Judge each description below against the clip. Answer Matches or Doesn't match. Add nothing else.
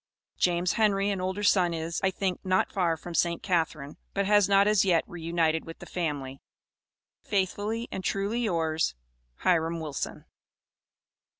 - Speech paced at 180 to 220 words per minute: Doesn't match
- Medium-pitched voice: Matches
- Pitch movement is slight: Doesn't match